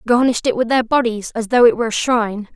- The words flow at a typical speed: No, fast, 260 wpm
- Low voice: No, high, 240 Hz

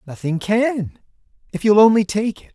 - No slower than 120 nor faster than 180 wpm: Yes, average, 140 wpm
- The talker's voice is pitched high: Yes, high, 200 Hz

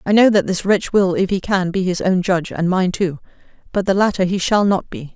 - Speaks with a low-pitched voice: No, high, 190 Hz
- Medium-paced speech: No, fast, 270 wpm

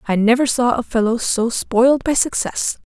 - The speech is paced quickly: No, average, 190 wpm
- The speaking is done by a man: No, female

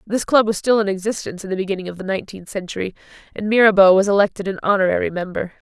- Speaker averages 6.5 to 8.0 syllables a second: Yes, 7.4 syllables/s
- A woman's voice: Yes, female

